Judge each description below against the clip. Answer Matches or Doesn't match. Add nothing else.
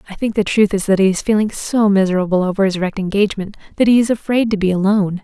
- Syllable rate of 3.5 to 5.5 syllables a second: Doesn't match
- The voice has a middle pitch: Doesn't match